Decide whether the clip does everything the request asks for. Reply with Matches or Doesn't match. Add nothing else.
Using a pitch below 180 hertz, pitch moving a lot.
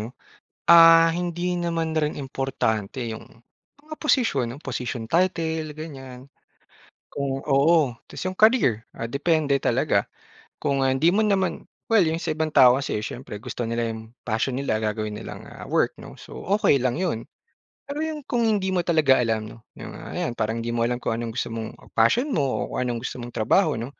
Matches